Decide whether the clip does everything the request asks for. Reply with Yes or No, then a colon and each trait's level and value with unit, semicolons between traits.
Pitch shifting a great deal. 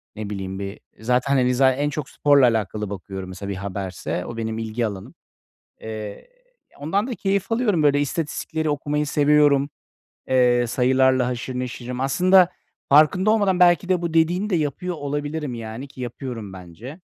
Yes: wide, 5.9 semitones